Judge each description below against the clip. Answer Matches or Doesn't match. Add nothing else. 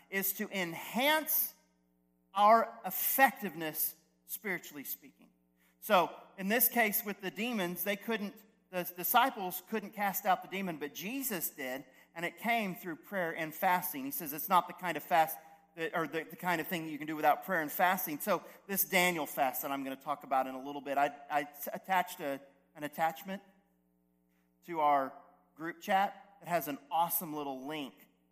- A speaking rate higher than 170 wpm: Matches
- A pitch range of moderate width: Matches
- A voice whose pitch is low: Doesn't match